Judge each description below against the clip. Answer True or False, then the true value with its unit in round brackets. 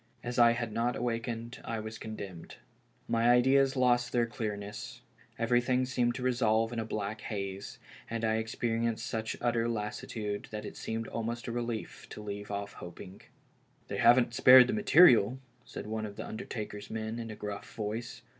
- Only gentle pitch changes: True (2.1 semitones)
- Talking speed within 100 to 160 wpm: False (175 wpm)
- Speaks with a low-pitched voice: True (115 Hz)